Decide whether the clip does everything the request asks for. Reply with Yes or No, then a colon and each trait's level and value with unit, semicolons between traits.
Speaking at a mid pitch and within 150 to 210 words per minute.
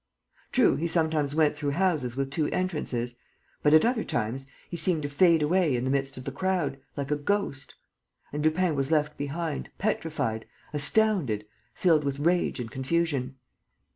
Yes: medium, 150 Hz; average, 170 wpm